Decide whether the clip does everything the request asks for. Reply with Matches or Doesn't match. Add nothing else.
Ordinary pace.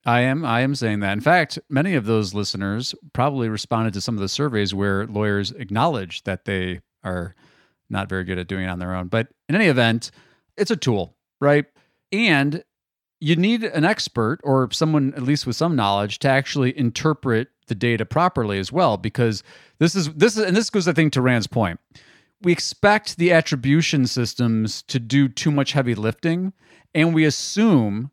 Matches